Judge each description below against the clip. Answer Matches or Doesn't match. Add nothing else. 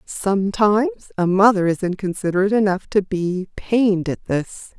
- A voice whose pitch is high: Matches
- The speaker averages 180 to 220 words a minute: Doesn't match